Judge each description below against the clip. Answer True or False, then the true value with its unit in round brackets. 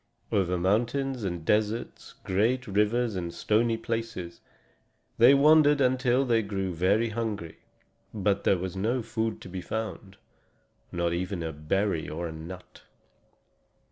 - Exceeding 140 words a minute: False (135 wpm)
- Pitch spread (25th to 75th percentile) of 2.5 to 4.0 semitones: False (4.4 semitones)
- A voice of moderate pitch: False (105 Hz)